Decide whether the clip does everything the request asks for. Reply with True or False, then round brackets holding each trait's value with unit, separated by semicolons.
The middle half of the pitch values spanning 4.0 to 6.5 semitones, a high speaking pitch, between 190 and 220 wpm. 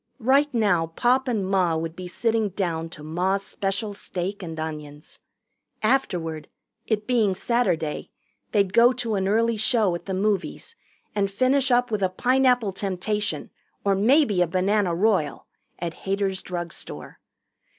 False (4.4 semitones; 200 Hz; 145 wpm)